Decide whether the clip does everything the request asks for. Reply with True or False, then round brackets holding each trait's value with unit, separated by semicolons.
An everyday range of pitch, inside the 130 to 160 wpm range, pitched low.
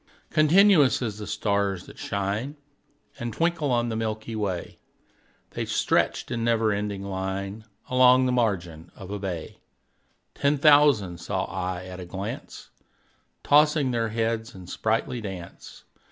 True (4.8 semitones; 140 wpm; 110 Hz)